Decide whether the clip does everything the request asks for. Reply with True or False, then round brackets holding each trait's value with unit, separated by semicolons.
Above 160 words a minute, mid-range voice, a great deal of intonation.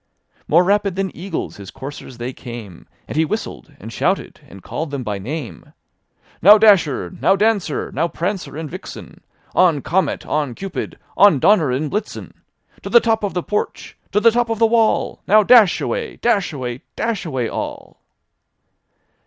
True (170 wpm; 180 Hz; 7.3 semitones)